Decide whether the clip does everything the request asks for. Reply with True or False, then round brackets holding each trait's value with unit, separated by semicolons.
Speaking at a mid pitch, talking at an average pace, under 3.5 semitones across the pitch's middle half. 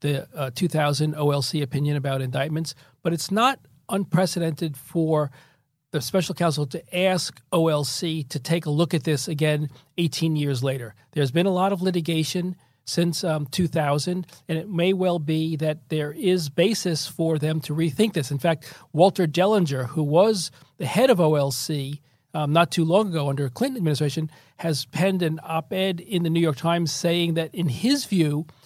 True (160 Hz; 180 wpm; 2.9 semitones)